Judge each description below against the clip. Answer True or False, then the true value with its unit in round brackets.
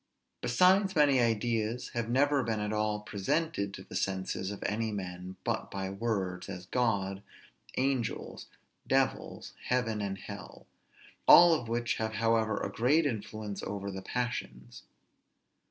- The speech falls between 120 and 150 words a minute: True (140 wpm)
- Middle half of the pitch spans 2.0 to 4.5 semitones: True (3.8 semitones)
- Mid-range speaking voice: False (110 Hz)